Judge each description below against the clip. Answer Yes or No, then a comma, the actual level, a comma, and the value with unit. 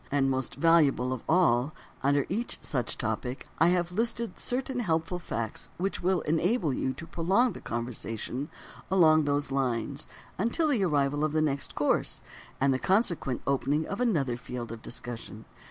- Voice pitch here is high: No, medium, 150 Hz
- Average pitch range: No, wide, 5.7 semitones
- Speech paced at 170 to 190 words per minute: No, average, 160 wpm